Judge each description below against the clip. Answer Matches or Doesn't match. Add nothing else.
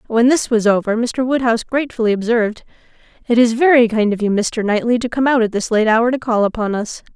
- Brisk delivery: Matches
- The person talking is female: Matches